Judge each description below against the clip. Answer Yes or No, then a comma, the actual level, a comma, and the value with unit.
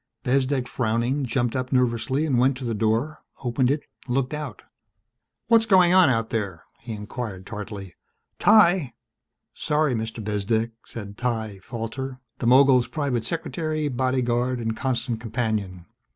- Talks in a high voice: No, low, 125 Hz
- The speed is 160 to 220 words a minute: No, slow, 135 wpm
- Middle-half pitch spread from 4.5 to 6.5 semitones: No, average, 3.4 semitones